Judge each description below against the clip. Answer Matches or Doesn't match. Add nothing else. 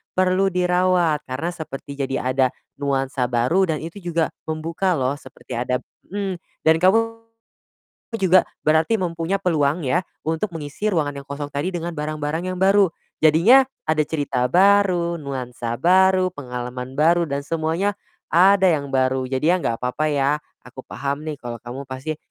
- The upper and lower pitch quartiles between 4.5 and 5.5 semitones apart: Matches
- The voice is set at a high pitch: Doesn't match